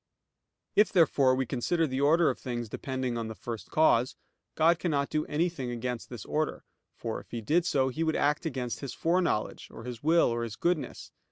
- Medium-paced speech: Yes, average, 195 wpm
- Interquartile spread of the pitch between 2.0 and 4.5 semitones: No, average, 5.0 semitones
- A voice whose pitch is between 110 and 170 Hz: Yes, low, 135 Hz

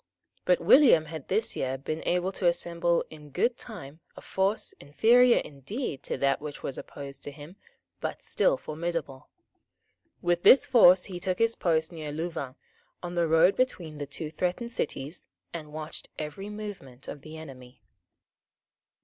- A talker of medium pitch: Yes, medium, 165 Hz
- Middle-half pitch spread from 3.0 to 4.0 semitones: No, average, 4.6 semitones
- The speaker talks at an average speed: Yes, average, 160 wpm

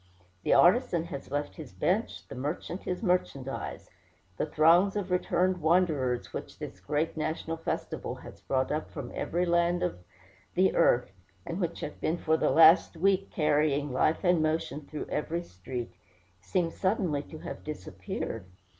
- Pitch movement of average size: Yes, average, 3.3 semitones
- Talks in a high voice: No, medium, 160 Hz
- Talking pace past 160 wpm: No, average, 155 wpm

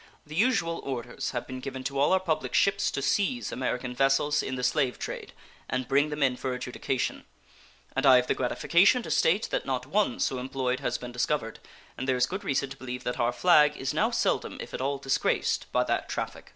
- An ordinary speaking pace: No, fast, 215 wpm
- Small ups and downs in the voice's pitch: No, average, 3.1 semitones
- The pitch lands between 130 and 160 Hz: Yes, low, 135 Hz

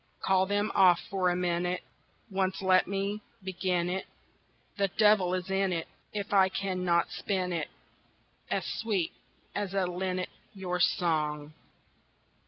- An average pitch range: No, narrow, 1.6 semitones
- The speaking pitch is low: No, medium, 185 Hz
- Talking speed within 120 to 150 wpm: Yes, average, 140 wpm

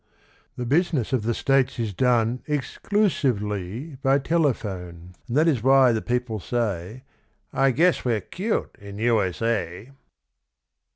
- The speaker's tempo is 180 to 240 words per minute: No, average, 155 wpm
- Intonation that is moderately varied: Yes, average, 4.5 semitones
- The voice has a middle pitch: No, low, 120 Hz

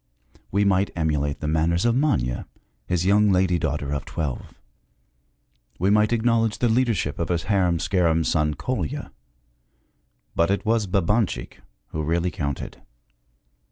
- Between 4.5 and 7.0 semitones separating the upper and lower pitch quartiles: Yes, average, 5.1 semitones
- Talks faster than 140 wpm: No, slow, 135 wpm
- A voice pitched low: Yes, very low, 90 Hz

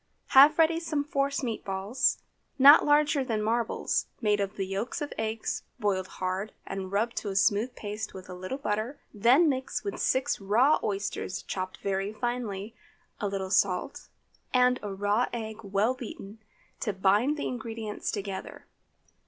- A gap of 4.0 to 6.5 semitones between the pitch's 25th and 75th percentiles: Yes, average, 4.6 semitones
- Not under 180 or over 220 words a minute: No, average, 160 wpm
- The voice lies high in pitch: Yes, high, 215 Hz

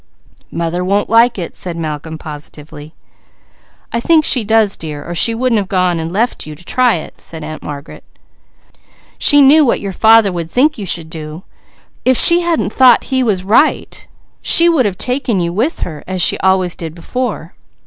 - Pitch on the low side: No, high, 190 Hz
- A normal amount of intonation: No, wide, 6.8 semitones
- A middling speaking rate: Yes, average, 175 wpm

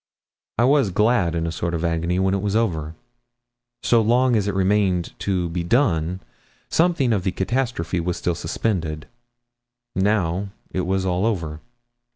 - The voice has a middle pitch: No, very low, 95 Hz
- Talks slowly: No, average, 160 wpm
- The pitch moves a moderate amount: Yes, average, 4.4 semitones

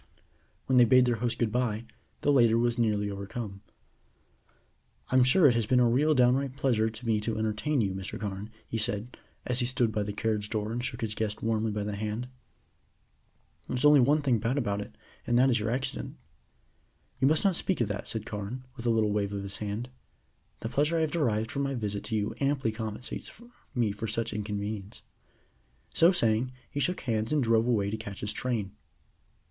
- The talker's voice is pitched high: No, low, 115 Hz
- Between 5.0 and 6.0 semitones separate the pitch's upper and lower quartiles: No, average, 3.3 semitones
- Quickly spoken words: Yes, fast, 210 wpm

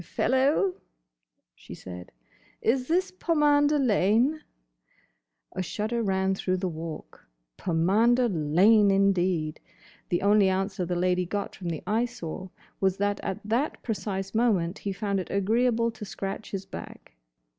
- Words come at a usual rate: No, slow, 130 wpm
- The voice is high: Yes, high, 200 Hz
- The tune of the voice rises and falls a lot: No, average, 4.1 semitones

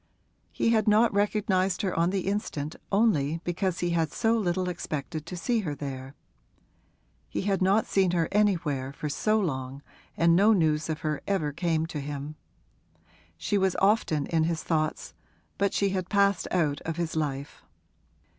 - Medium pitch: Yes, medium, 175 Hz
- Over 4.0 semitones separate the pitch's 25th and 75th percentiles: Yes, average, 4.5 semitones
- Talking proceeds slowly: No, average, 165 wpm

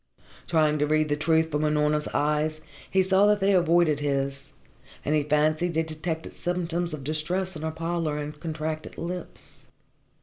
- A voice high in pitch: No, medium, 155 Hz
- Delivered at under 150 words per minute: No, average, 165 wpm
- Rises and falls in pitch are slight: Yes, narrow, 2.3 semitones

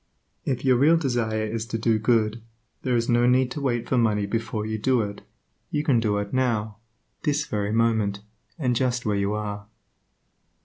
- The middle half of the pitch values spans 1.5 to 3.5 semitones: Yes, average, 2.8 semitones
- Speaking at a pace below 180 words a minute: No, average, 185 wpm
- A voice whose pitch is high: No, low, 115 Hz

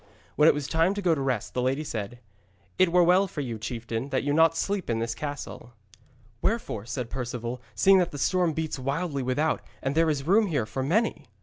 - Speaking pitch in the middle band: Yes, medium, 145 Hz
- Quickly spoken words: Yes, fast, 215 wpm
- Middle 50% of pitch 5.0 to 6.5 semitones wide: Yes, wide, 5.4 semitones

